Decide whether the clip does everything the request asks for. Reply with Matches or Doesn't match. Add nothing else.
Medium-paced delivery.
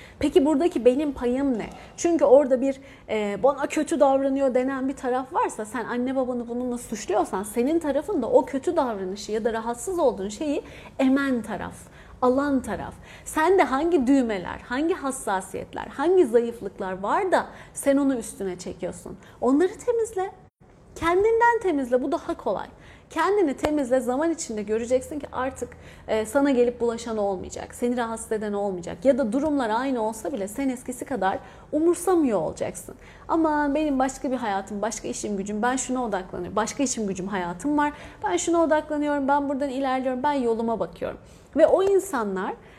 Doesn't match